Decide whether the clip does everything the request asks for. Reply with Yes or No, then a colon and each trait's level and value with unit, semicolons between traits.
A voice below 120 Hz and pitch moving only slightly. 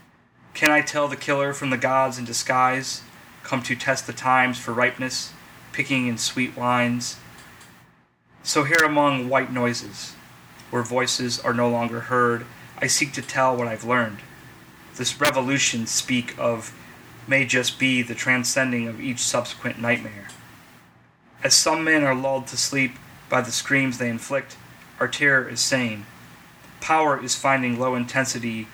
No: low, 125 Hz; narrow, 2.1 semitones